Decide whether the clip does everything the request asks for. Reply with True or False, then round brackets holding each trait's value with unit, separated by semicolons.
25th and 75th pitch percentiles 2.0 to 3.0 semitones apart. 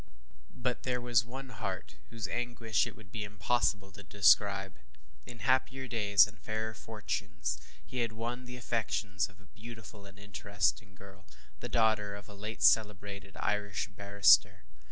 True (2.6 semitones)